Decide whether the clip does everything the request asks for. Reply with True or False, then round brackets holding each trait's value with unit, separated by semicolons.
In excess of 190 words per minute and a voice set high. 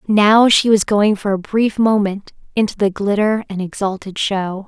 False (180 wpm; 205 Hz)